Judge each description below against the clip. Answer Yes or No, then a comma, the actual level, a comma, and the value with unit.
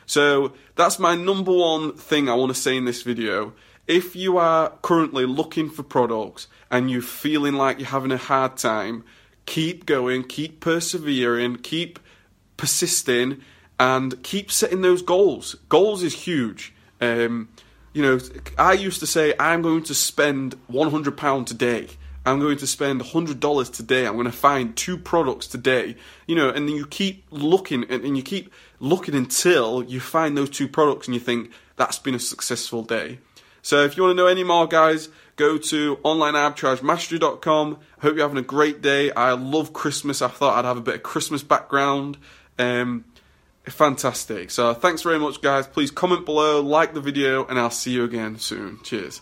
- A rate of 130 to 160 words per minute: No, average, 180 wpm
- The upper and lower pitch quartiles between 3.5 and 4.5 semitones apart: Yes, average, 4.2 semitones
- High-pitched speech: No, medium, 140 Hz